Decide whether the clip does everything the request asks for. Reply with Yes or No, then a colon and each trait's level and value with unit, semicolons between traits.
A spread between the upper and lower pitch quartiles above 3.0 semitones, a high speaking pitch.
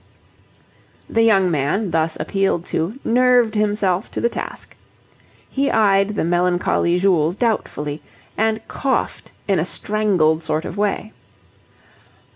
Yes: average, 4.3 semitones; high, 195 Hz